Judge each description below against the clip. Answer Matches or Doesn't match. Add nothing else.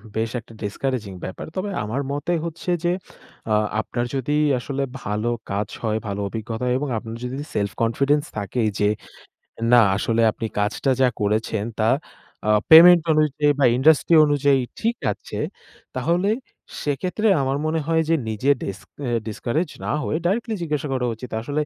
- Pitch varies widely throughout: Matches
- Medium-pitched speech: Doesn't match